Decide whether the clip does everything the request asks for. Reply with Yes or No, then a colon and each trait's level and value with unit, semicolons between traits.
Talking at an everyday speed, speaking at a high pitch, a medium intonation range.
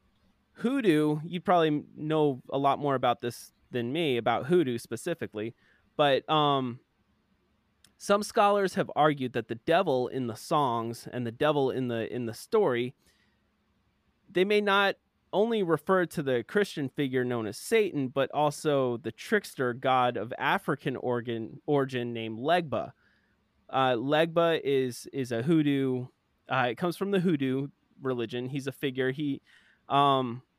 No: average, 145 wpm; low, 135 Hz; average, 4.9 semitones